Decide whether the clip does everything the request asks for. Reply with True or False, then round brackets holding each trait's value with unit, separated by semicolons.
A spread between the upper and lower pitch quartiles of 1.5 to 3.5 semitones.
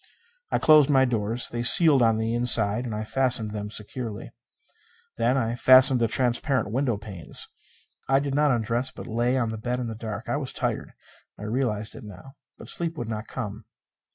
True (3.2 semitones)